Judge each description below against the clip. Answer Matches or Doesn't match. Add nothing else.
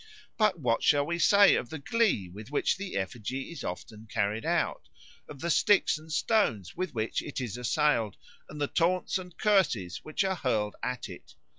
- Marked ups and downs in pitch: Matches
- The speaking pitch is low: Doesn't match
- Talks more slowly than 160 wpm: Doesn't match